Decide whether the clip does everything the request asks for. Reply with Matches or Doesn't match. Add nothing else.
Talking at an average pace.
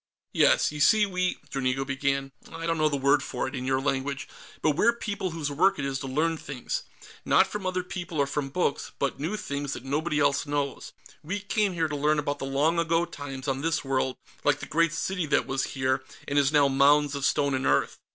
Doesn't match